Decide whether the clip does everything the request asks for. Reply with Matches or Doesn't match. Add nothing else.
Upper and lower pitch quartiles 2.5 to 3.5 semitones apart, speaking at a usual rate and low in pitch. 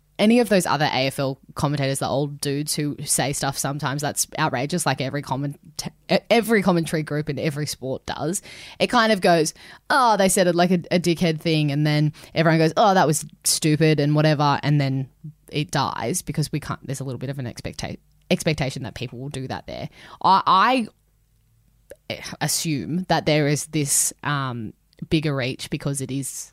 Doesn't match